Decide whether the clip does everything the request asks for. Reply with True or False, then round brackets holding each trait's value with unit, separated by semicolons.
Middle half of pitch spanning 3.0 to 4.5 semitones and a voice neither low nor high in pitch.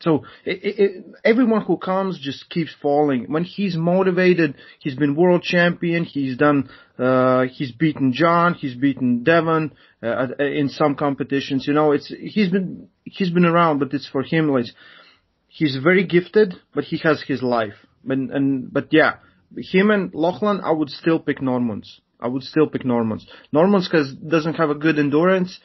True (4.2 semitones; 155 Hz)